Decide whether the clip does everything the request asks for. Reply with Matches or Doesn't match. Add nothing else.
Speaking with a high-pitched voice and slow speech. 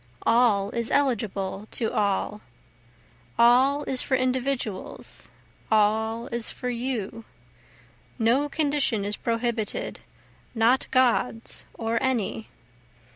Matches